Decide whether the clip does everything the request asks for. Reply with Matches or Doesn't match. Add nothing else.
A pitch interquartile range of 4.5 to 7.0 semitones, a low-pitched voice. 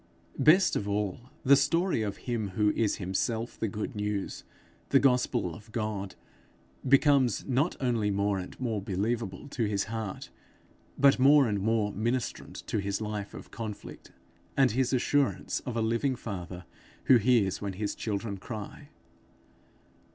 Doesn't match